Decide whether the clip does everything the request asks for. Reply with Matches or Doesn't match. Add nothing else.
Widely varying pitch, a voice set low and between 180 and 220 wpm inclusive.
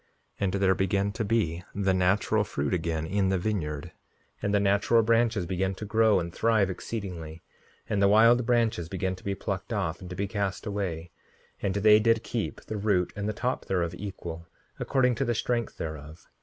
Doesn't match